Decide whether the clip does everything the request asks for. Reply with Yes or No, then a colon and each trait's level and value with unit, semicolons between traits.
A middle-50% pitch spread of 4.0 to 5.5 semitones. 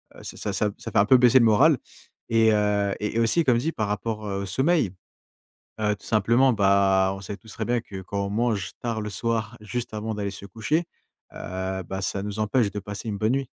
No: average, 2.7 semitones